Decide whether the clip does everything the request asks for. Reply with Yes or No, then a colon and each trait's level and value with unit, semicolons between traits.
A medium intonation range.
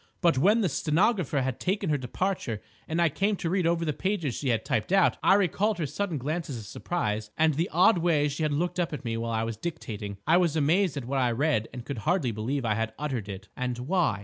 No: wide, 6.4 semitones